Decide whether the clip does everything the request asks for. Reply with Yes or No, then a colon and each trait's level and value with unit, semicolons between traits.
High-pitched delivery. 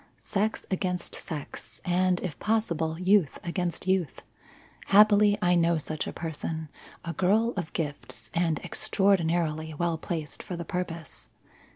No: medium, 175 Hz